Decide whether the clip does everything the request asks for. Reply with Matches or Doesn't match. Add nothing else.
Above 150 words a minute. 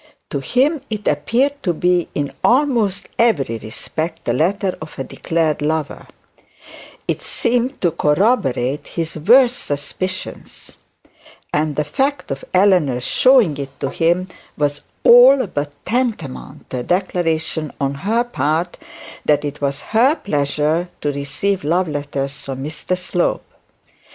Doesn't match